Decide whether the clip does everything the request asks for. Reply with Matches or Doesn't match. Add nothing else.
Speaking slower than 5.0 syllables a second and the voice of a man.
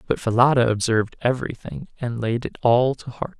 Doesn't match